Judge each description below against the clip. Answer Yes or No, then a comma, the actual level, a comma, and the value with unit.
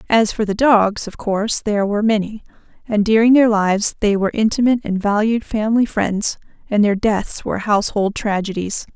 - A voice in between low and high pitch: No, high, 215 Hz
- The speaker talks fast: No, average, 175 wpm